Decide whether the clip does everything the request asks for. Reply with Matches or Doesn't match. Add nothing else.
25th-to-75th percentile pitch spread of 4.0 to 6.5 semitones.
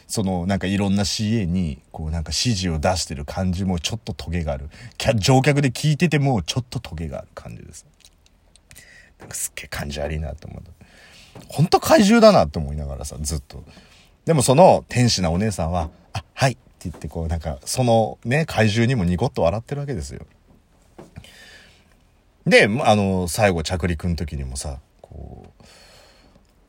Matches